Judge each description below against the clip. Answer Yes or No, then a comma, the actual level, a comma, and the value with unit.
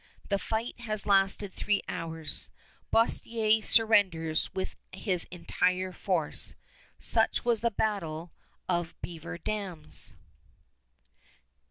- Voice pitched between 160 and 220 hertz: Yes, high, 190 Hz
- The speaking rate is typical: No, slow, 95 wpm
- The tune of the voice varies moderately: Yes, average, 4.3 semitones